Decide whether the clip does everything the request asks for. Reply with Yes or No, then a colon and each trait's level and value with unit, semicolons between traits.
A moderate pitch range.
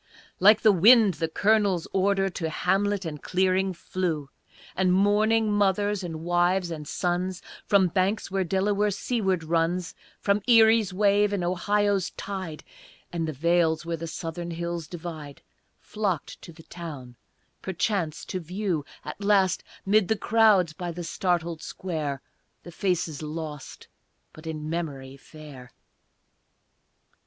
Yes: average, 3.6 semitones